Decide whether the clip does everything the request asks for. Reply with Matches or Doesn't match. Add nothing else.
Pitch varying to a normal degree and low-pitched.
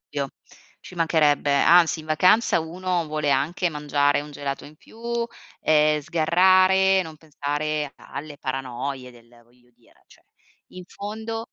Doesn't match